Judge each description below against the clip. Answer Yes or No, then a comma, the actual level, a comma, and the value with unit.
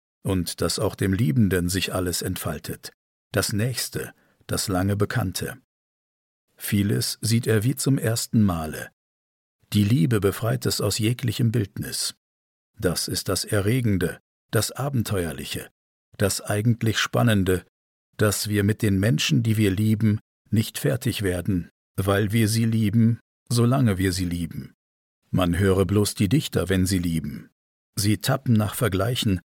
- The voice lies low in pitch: Yes, low, 105 Hz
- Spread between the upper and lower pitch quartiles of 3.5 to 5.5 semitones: Yes, average, 3.9 semitones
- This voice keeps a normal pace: Yes, average, 135 wpm